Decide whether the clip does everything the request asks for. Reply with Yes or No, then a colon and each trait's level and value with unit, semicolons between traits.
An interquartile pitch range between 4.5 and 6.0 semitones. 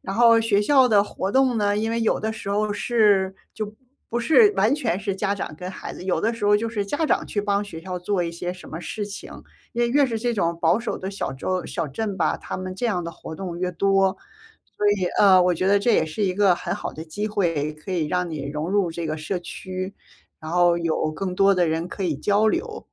No: average, 3.4 semitones